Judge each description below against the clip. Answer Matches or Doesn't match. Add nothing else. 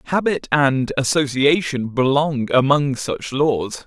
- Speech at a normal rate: Doesn't match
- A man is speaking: Matches